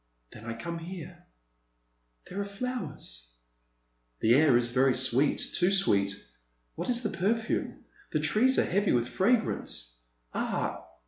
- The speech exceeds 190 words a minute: No, slow, 135 wpm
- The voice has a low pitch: No, medium, 170 Hz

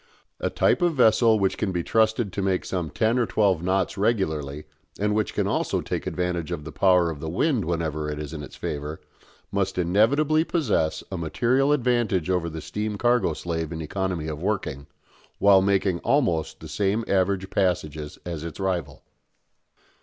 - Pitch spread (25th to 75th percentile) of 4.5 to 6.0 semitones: Yes, average, 4.9 semitones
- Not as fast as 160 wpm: No, average, 175 wpm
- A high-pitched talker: No, very low, 95 Hz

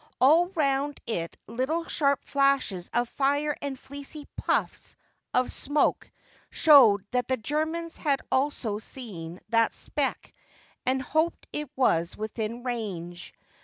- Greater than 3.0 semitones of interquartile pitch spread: Yes, average, 4.8 semitones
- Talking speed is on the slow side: Yes, slow, 125 wpm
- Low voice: No, very high, 265 Hz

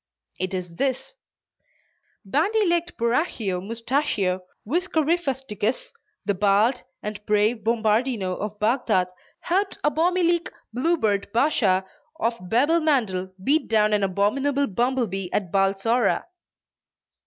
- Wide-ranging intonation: Yes, wide, 6.3 semitones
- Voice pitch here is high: Yes, high, 230 Hz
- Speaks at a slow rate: Yes, slow, 95 wpm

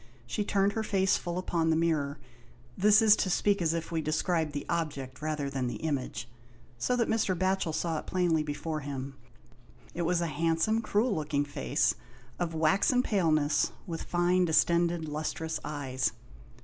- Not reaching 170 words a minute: No, average, 175 wpm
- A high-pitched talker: No, medium, 165 Hz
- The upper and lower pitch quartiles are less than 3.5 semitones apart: No, average, 3.8 semitones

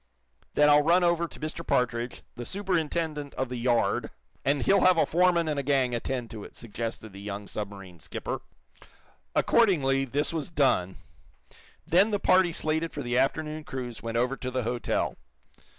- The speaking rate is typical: Yes, average, 170 wpm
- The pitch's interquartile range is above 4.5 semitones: Yes, wide, 5.5 semitones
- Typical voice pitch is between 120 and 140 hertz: Yes, low, 135 Hz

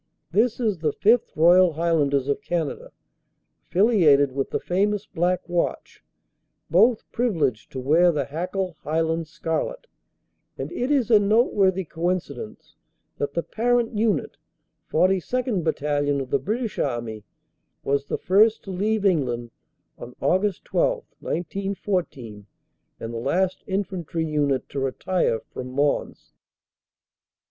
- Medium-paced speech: No, slow, 125 wpm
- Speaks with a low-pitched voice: No, medium, 175 Hz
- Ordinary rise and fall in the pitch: No, wide, 6.1 semitones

